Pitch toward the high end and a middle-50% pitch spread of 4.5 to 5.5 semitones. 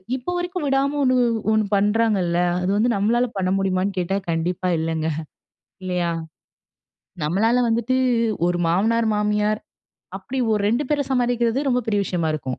Yes: high, 210 Hz; average, 5.0 semitones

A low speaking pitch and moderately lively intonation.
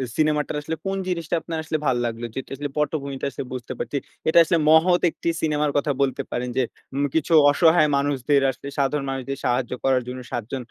No: medium, 145 Hz; average, 3.2 semitones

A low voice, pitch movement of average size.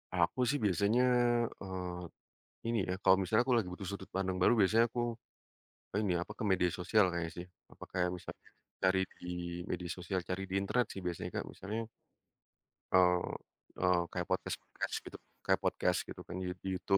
No: very low, 95 Hz; narrow, 2.0 semitones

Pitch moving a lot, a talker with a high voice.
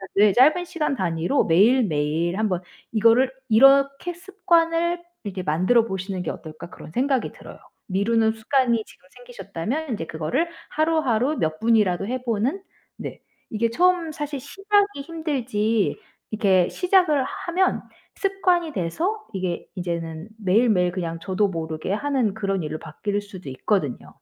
Yes: wide, 8.1 semitones; high, 225 Hz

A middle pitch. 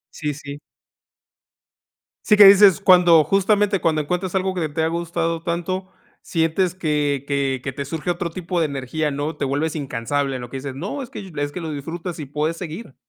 Yes: medium, 160 Hz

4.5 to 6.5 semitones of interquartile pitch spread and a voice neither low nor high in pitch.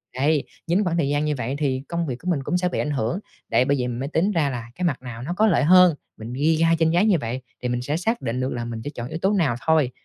Yes: average, 5.2 semitones; medium, 145 Hz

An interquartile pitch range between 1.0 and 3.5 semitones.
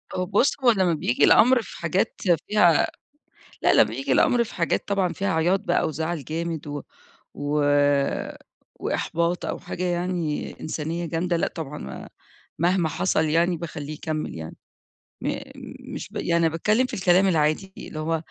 Yes: average, 2.9 semitones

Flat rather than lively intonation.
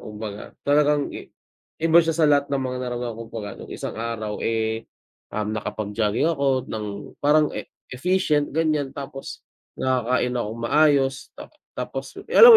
No: average, 4.7 semitones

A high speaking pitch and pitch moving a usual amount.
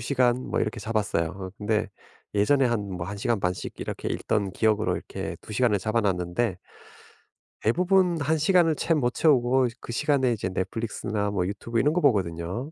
No: low, 115 Hz; average, 4.9 semitones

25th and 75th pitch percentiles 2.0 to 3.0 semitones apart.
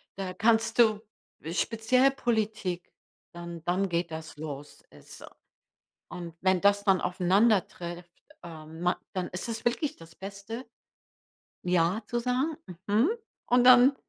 No: average, 4.9 semitones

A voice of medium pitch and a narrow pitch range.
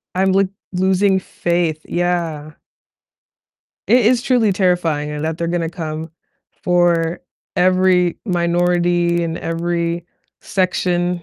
Yes: medium, 175 Hz; narrow, 1.6 semitones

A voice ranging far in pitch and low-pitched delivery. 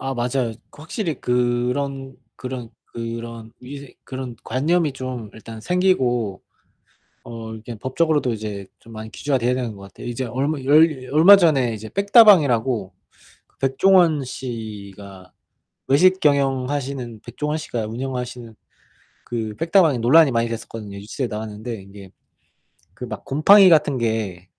No: average, 4.1 semitones; low, 125 Hz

